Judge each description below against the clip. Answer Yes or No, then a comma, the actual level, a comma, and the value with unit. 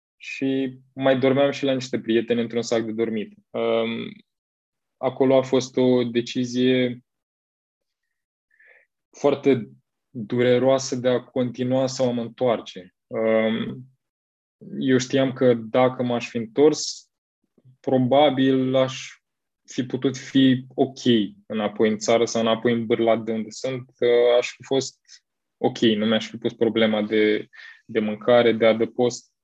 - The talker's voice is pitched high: No, low, 125 Hz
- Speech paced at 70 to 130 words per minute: Yes, average, 125 wpm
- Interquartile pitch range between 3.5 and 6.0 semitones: No, narrow, 2.5 semitones